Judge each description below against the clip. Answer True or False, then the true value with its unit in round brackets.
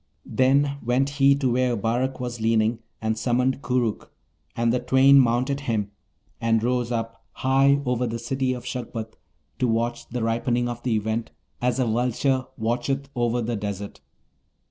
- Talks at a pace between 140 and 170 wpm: True (160 wpm)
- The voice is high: False (120 Hz)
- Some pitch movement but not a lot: False (2.3 semitones)